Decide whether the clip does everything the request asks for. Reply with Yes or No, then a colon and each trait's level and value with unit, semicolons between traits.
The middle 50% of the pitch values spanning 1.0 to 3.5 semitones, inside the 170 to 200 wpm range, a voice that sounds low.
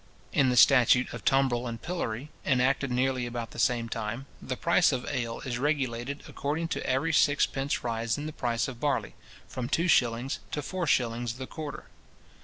Yes: average, 3.2 semitones; average, 180 wpm; low, 130 Hz